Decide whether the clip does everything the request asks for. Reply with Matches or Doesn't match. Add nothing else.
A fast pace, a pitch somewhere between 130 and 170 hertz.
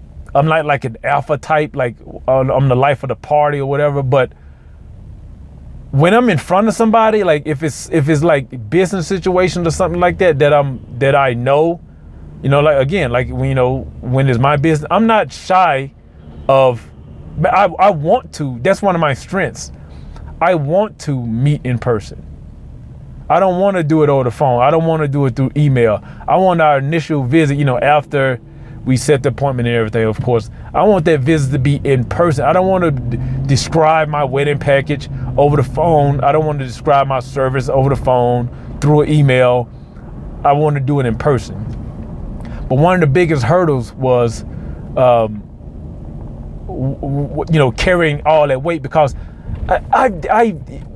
Doesn't match